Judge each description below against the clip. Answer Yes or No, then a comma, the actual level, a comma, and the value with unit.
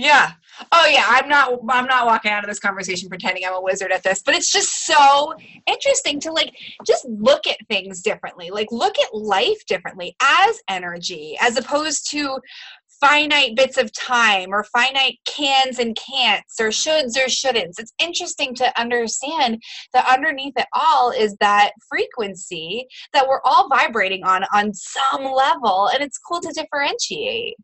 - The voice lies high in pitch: Yes, very high, 260 Hz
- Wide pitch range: Yes, wide, 5.7 semitones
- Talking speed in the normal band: Yes, average, 165 wpm